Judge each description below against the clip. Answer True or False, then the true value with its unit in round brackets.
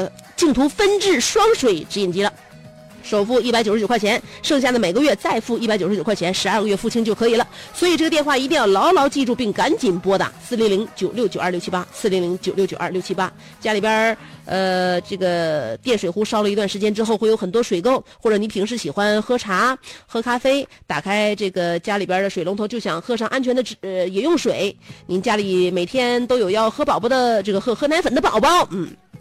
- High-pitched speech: True (215 Hz)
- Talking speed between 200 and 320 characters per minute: False (335 characters per minute)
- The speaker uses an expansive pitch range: False (4.3 semitones)